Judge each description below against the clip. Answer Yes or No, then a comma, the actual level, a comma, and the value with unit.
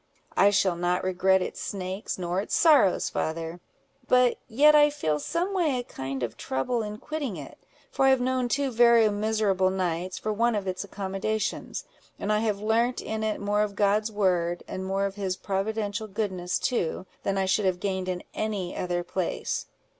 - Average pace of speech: Yes, average, 185 wpm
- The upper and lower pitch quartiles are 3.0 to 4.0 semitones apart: Yes, average, 3.3 semitones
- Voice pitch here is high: Yes, high, 200 Hz